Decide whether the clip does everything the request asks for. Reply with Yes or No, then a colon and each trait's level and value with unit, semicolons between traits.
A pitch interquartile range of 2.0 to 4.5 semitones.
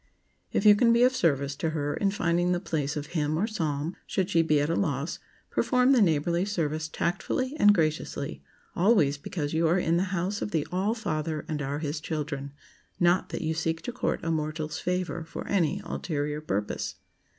Yes: average, 4.0 semitones